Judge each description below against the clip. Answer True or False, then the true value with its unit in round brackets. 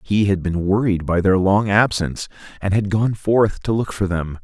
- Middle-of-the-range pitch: False (100 Hz)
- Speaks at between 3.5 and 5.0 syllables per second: True (4.8 syllables/s)